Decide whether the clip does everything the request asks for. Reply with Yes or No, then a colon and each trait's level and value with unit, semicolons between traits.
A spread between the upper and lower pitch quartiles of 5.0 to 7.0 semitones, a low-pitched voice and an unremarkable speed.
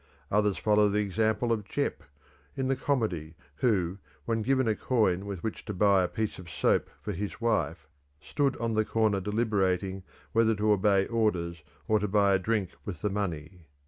No: average, 2.8 semitones; low, 105 Hz; average, 180 wpm